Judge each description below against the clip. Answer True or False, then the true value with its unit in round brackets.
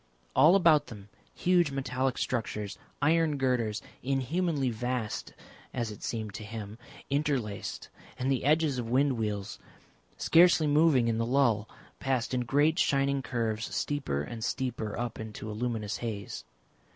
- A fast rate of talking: False (140 wpm)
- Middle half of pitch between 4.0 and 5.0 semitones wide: True (4.4 semitones)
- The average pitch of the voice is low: True (125 Hz)